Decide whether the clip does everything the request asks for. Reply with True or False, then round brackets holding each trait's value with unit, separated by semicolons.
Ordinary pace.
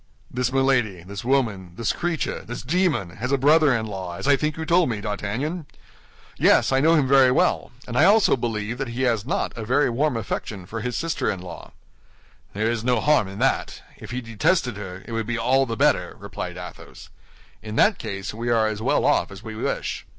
False (215 wpm)